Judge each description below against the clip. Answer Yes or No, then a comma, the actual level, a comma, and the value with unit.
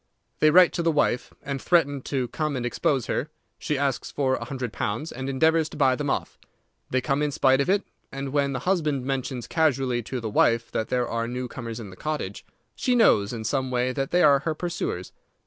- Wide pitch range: No, average, 3.4 semitones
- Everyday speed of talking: No, fast, 220 wpm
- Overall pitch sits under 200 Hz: Yes, low, 135 Hz